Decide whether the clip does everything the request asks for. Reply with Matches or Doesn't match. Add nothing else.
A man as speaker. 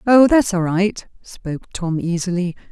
Doesn't match